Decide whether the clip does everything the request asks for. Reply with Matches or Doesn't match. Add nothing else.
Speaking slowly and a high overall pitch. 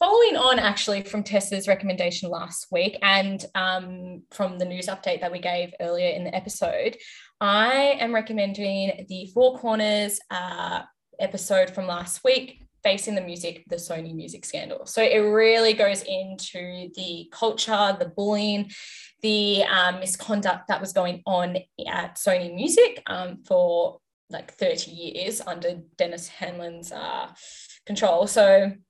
Doesn't match